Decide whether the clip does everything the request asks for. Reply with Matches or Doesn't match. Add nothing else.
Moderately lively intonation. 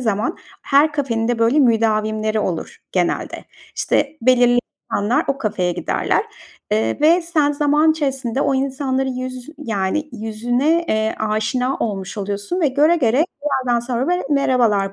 Matches